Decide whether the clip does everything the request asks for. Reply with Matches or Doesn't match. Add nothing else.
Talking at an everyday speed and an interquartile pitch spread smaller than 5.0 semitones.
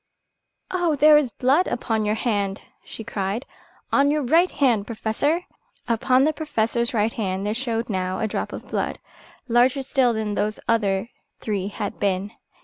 Matches